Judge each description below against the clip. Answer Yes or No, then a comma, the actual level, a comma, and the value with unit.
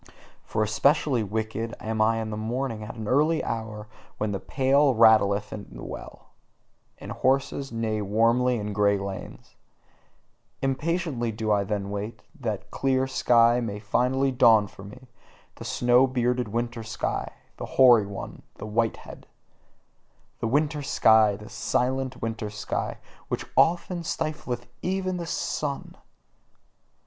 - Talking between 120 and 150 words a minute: Yes, average, 140 wpm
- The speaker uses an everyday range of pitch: Yes, average, 3.6 semitones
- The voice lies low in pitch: Yes, low, 115 Hz